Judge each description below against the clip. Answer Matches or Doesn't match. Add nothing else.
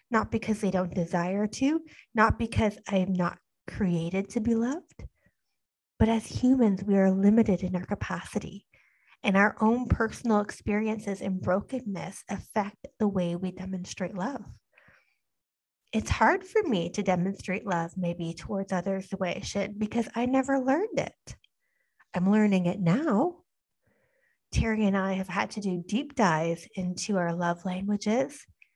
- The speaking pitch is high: Matches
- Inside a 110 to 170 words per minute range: Matches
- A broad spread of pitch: Doesn't match